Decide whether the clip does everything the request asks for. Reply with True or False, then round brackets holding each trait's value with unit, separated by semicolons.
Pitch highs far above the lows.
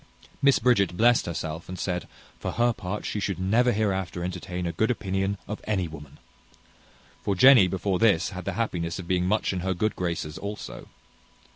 False (3.4 semitones)